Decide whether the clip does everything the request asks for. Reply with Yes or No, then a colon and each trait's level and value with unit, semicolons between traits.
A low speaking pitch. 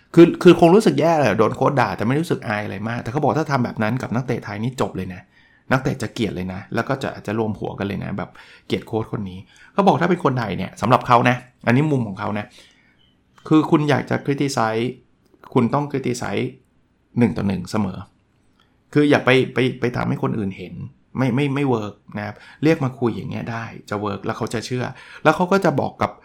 Yes: low, 120 Hz